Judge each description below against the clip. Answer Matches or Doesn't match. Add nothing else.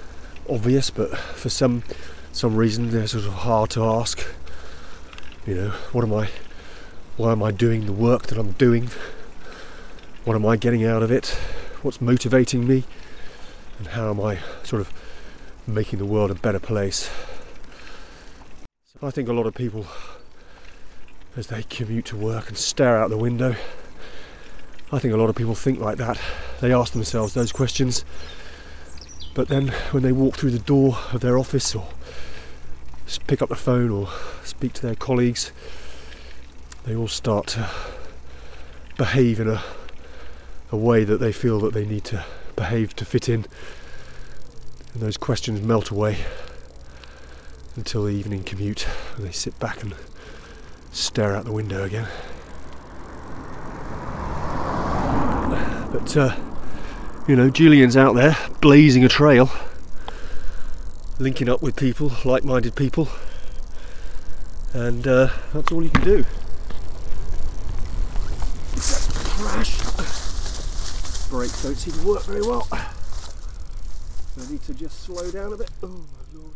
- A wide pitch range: Matches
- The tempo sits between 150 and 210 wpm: Doesn't match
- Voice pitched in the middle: Doesn't match